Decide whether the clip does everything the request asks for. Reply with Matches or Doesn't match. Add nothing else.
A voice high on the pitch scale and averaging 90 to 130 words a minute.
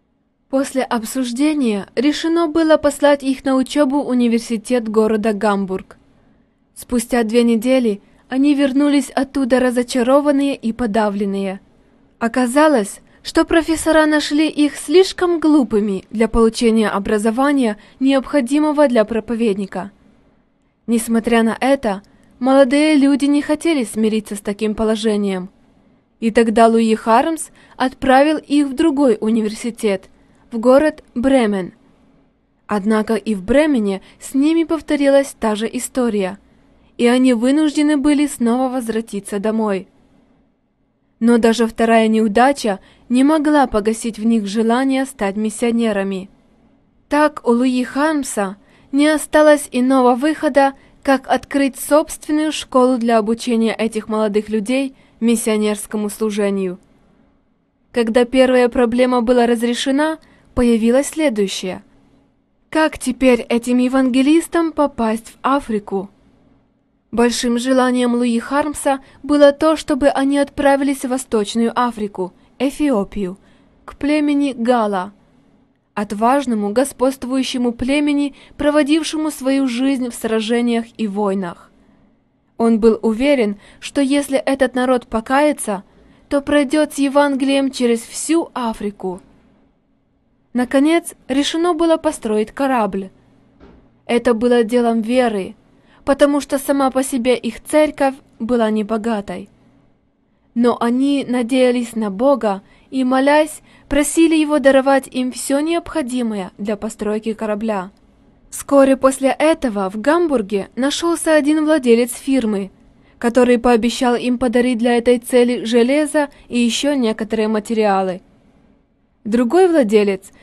Matches